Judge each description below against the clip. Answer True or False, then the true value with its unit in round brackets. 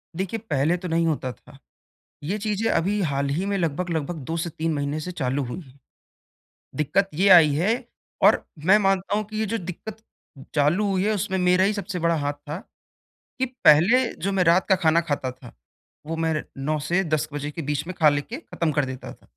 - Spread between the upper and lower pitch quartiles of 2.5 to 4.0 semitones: False (4.6 semitones)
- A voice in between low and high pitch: True (170 Hz)